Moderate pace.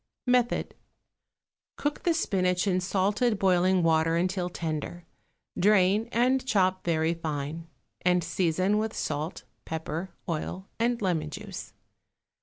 No: slow, 115 wpm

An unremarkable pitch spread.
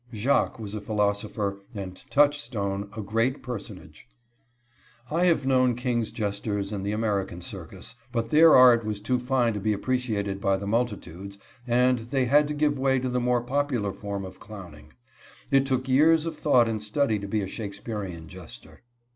Yes: average, 4.2 semitones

